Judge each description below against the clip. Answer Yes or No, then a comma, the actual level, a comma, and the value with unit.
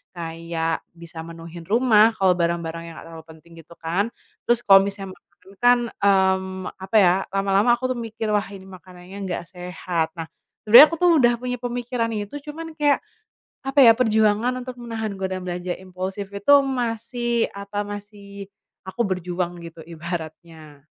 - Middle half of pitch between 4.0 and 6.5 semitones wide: Yes, average, 4.8 semitones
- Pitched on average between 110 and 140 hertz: No, high, 195 Hz